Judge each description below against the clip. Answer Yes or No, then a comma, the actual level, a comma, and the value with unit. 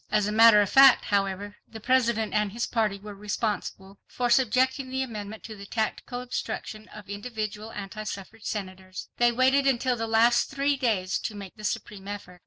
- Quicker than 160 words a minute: Yes, average, 185 wpm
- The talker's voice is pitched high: Yes, high, 215 Hz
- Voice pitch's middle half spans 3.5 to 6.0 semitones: No, average, 3.0 semitones